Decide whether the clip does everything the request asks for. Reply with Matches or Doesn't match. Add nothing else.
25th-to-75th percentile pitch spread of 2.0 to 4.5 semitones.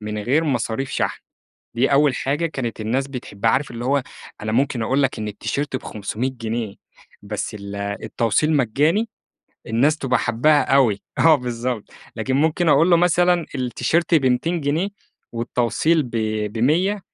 Doesn't match